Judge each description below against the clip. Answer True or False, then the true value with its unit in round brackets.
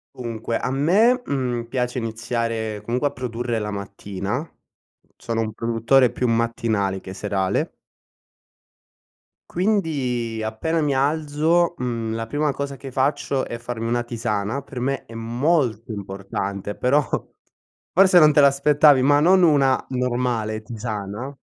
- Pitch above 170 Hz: False (120 Hz)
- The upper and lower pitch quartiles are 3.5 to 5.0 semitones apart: True (4.1 semitones)